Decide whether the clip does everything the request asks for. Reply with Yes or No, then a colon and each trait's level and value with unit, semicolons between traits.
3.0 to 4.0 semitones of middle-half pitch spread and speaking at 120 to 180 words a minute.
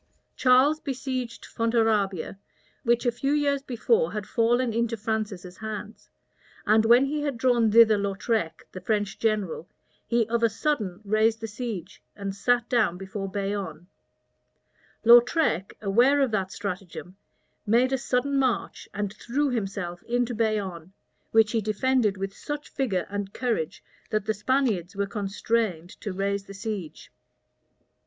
Yes: average, 3.6 semitones; average, 140 wpm